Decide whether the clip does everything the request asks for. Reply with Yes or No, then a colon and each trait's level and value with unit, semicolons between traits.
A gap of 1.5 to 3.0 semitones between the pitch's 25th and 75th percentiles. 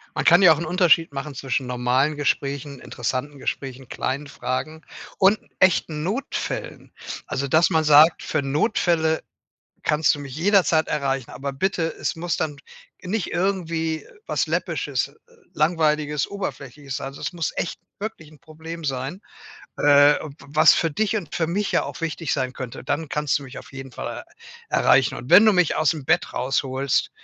No: average, 3.5 semitones